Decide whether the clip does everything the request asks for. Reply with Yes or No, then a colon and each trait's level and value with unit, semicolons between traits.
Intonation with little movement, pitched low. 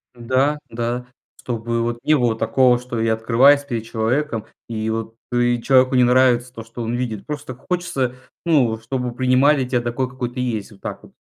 Yes: narrow, 2.1 semitones; low, 125 Hz